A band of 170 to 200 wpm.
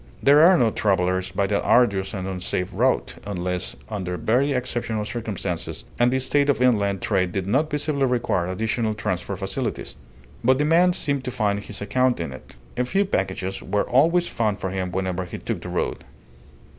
Yes: average, 180 wpm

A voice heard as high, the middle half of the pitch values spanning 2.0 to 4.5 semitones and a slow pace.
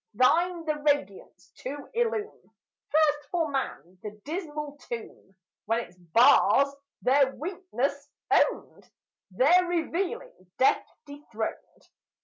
No: very high, 290 Hz; wide, 5.4 semitones; slow, 105 wpm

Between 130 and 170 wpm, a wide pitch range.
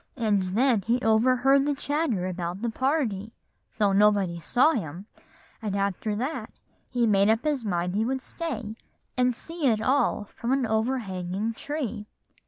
No: average, 155 wpm; average, 4.6 semitones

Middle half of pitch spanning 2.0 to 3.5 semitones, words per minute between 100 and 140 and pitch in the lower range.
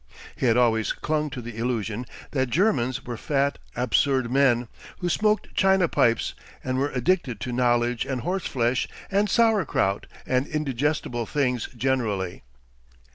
No: average, 4.0 semitones; slow, 135 wpm; low, 130 Hz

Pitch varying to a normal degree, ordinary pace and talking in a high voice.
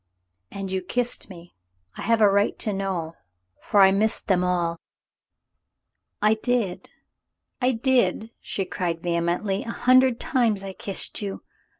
Yes: average, 4.1 semitones; average, 155 wpm; high, 195 Hz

